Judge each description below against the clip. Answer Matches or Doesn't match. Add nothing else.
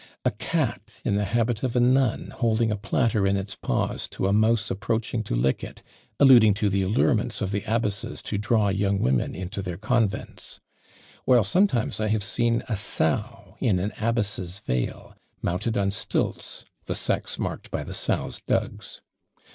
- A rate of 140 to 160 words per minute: Doesn't match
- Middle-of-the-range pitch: Doesn't match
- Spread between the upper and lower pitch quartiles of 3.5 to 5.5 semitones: Doesn't match